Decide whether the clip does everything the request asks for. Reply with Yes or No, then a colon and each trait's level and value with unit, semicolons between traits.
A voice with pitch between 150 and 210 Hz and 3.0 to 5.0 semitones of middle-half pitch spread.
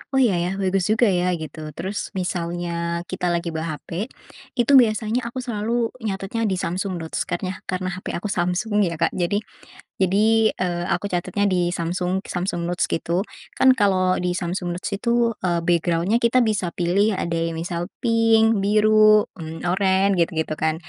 Yes: medium, 185 Hz; average, 3.5 semitones